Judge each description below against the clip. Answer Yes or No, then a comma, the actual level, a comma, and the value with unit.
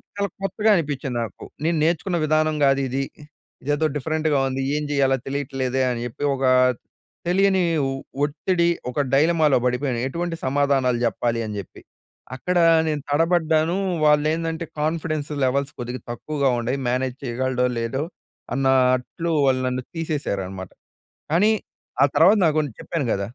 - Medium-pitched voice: Yes, medium, 145 Hz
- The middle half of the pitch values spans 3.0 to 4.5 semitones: Yes, average, 3.9 semitones